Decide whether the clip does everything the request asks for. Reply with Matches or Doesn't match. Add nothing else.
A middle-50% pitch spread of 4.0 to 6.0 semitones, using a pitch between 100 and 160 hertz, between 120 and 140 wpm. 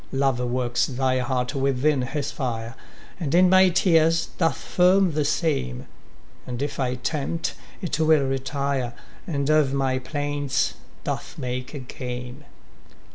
Doesn't match